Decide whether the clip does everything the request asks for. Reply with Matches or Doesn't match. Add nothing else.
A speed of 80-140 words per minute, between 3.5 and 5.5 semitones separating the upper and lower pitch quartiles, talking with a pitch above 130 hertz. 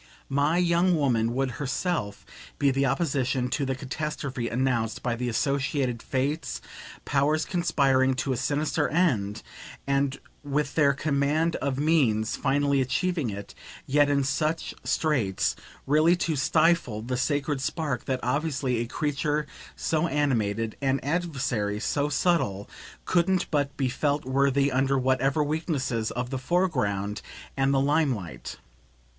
Doesn't match